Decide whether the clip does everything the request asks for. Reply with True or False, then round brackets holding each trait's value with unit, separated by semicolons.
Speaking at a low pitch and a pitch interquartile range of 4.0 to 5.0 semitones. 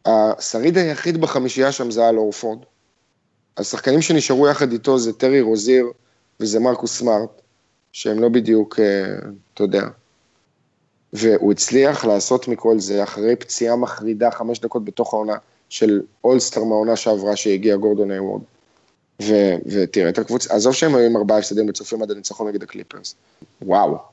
False (115 Hz; 2.9 semitones)